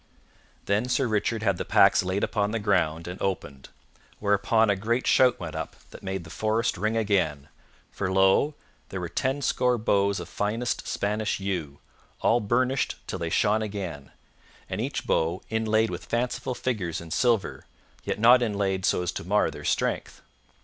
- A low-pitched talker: Yes, low, 100 Hz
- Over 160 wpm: Yes, average, 170 wpm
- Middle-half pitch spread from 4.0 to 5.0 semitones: No, average, 3.5 semitones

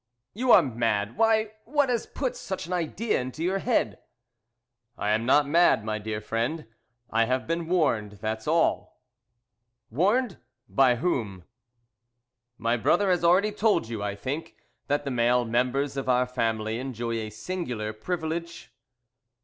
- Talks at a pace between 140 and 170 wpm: Yes, average, 150 wpm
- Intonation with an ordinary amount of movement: No, wide, 7.6 semitones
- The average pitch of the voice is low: Yes, low, 130 Hz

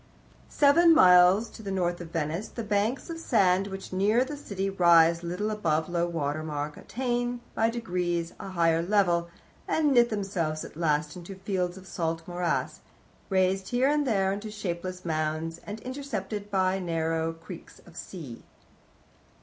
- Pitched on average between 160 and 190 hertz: Yes, medium, 185 Hz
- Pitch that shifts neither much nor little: Yes, average, 4.0 semitones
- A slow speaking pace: No, average, 160 wpm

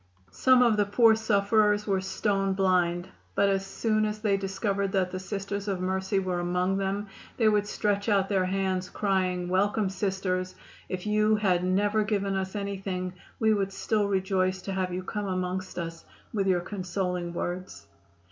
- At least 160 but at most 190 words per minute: Yes, average, 170 wpm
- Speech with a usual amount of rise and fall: No, narrow, 1.8 semitones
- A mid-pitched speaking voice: No, high, 195 Hz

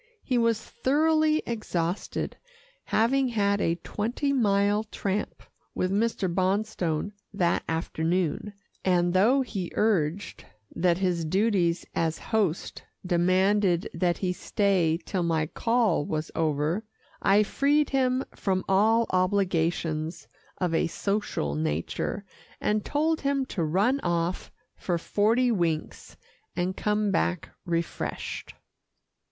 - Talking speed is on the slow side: Yes, slow, 115 wpm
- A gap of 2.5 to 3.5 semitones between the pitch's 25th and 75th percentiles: No, average, 4.4 semitones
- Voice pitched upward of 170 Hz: Yes, high, 190 Hz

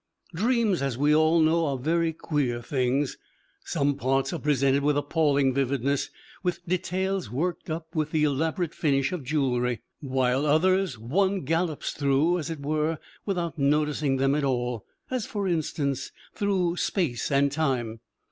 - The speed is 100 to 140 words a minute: No, average, 150 wpm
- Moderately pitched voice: Yes, medium, 150 Hz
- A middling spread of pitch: Yes, average, 3.6 semitones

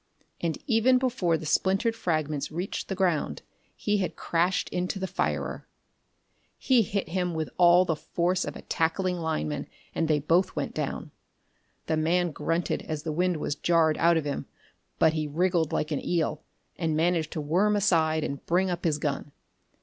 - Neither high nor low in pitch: Yes, medium, 170 Hz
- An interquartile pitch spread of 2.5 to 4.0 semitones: Yes, average, 2.8 semitones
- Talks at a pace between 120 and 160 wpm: No, average, 175 wpm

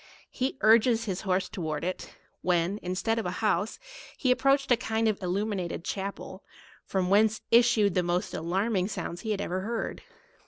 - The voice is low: No, high, 200 Hz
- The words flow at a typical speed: Yes, average, 180 wpm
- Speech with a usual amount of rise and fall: Yes, average, 3.6 semitones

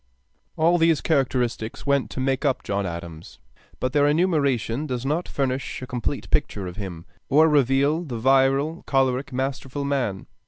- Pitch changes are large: No, average, 3.1 semitones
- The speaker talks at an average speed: Yes, average, 160 wpm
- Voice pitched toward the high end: No, low, 135 Hz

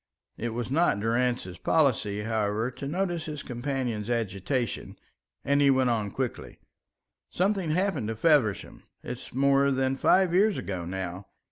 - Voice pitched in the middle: No, low, 125 Hz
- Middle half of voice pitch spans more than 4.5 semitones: Yes, average, 4.9 semitones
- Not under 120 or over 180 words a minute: Yes, average, 140 wpm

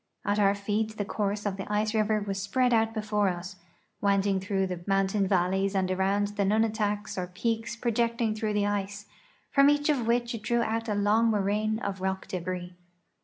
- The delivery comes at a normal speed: Yes, average, 190 wpm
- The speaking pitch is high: Yes, high, 205 Hz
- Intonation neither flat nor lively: No, narrow, 2.3 semitones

